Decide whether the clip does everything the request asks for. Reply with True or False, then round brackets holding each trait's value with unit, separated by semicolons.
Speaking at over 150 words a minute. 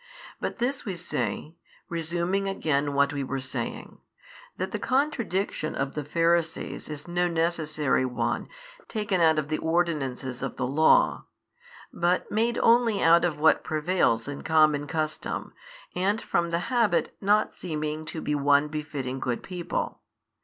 False (145 wpm)